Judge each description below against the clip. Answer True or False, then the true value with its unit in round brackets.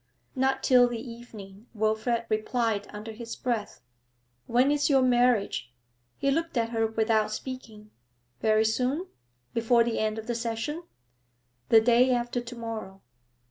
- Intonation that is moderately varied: False (2.3 semitones)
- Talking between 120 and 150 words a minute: True (140 wpm)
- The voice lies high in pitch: True (230 Hz)